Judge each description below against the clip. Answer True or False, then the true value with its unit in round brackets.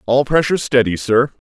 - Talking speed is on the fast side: False (165 wpm)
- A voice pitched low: True (125 Hz)